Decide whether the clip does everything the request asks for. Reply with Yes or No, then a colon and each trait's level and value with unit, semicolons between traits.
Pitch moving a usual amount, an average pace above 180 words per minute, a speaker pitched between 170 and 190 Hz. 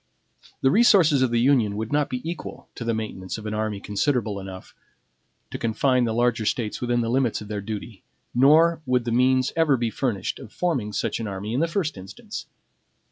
No: average, 4.1 semitones; average, 200 wpm; low, 120 Hz